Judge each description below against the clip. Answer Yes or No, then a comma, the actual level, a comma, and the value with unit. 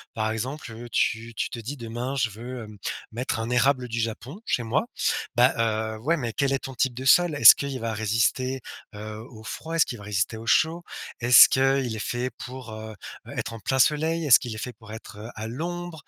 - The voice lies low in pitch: Yes, low, 120 Hz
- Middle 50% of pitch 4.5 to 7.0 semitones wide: No, average, 3.3 semitones